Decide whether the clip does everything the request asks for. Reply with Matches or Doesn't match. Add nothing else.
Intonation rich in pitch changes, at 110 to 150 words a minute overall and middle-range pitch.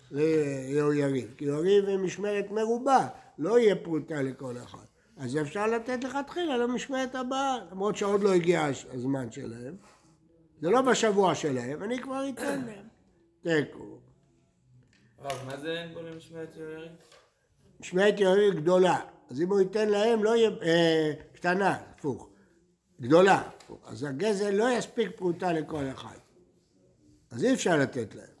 Matches